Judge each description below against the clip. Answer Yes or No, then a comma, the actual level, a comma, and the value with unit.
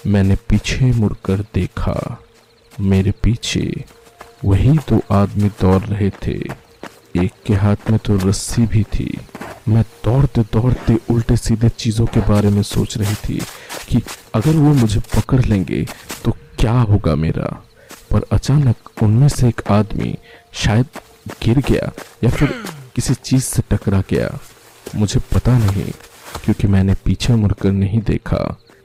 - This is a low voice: Yes, low, 110 Hz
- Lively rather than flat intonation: No, average, 3.2 semitones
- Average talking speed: Yes, average, 140 wpm